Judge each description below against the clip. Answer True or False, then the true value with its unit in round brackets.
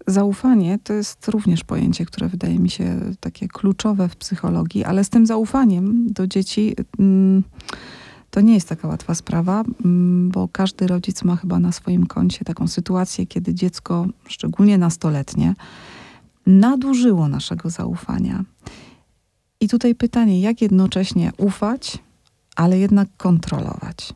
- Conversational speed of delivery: True (125 wpm)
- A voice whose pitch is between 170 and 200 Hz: True (190 Hz)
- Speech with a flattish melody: False (3.1 semitones)